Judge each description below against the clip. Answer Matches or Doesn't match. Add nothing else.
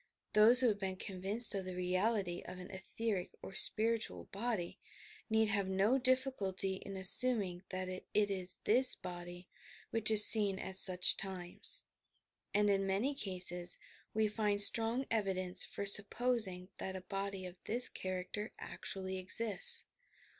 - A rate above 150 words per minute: Doesn't match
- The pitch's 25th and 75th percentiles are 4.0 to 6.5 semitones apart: Doesn't match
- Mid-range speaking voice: Doesn't match